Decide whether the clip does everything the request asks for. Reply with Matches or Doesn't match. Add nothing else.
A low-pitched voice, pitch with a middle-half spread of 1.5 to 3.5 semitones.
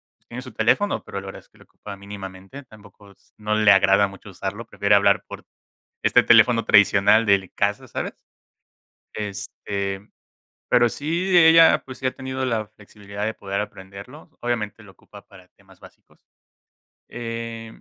Matches